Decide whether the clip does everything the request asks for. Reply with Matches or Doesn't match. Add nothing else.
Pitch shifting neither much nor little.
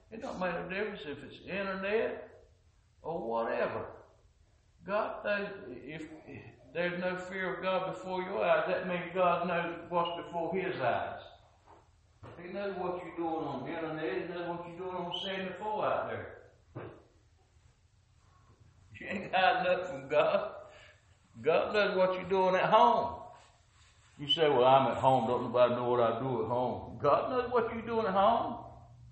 Doesn't match